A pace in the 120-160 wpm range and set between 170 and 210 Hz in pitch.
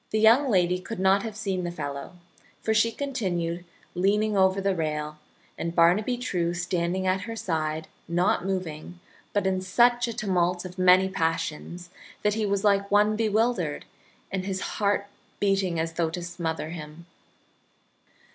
Yes: average, 155 wpm; medium, 185 Hz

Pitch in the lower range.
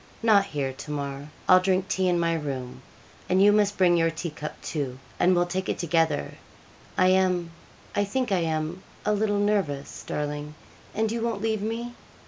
No: medium, 180 Hz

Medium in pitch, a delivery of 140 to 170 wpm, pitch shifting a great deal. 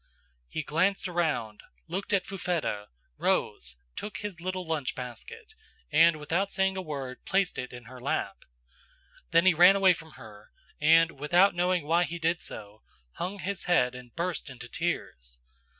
Yes: medium, 165 Hz; average, 160 wpm; wide, 6.2 semitones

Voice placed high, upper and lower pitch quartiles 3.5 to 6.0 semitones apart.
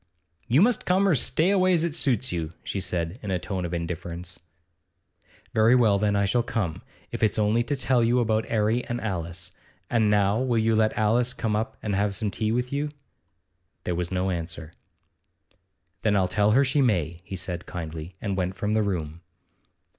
No: low, 105 Hz; average, 4.8 semitones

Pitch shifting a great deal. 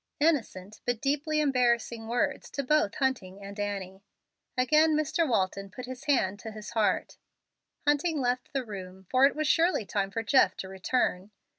Yes: wide, 6.3 semitones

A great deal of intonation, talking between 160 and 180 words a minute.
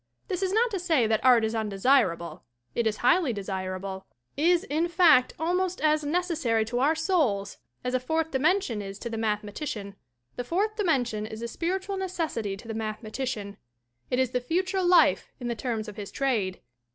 No: wide, 7.8 semitones; average, 190 wpm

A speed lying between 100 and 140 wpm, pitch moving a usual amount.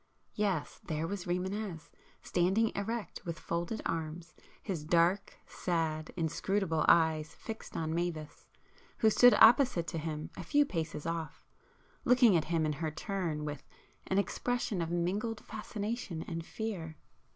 Yes: slow, 135 wpm; average, 4.3 semitones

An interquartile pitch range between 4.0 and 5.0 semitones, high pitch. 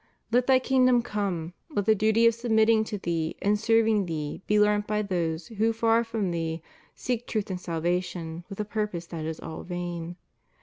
Yes: average, 4.6 semitones; high, 205 Hz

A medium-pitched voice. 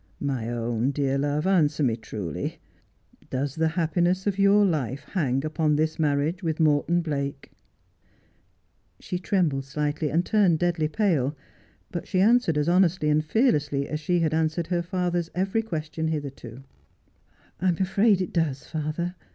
Yes: medium, 160 Hz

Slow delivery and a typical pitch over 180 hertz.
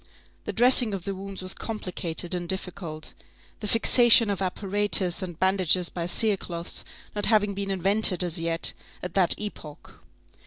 No: average, 150 wpm; high, 190 Hz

